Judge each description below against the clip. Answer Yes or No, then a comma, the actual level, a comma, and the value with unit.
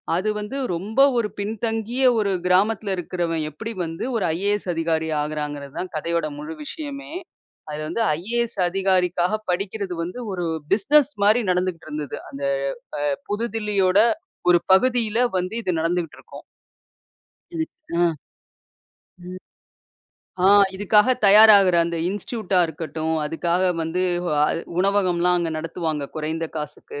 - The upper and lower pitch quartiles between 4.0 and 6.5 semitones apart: Yes, average, 4.3 semitones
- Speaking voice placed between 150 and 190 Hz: Yes, medium, 185 Hz